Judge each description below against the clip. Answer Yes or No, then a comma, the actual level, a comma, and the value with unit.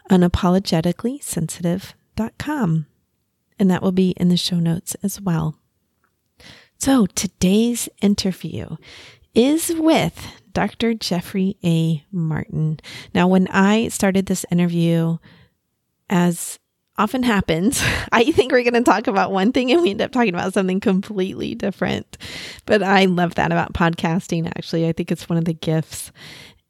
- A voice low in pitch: No, medium, 185 Hz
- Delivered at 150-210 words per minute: No, average, 140 wpm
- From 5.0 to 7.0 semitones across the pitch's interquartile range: No, average, 3.9 semitones